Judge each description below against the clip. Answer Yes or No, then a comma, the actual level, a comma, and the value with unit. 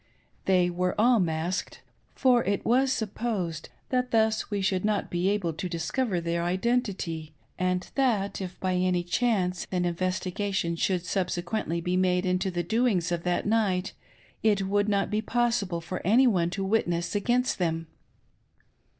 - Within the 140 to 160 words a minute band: Yes, average, 155 wpm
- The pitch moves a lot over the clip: No, average, 3.6 semitones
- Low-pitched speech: No, medium, 185 Hz